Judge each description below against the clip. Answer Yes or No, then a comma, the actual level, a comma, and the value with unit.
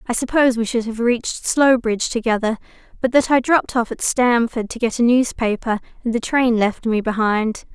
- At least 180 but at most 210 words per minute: Yes, average, 195 wpm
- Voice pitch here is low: No, high, 235 Hz